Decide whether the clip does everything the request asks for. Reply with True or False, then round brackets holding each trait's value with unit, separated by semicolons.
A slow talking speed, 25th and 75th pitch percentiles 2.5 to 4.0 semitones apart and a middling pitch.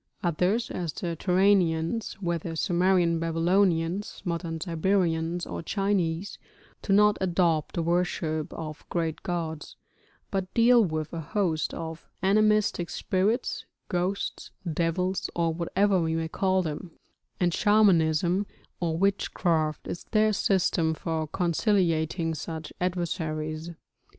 True (115 wpm; 2.9 semitones; 175 Hz)